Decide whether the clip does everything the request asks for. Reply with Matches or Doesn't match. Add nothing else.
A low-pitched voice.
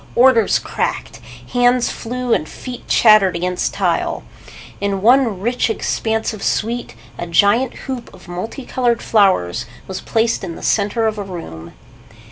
Doesn't match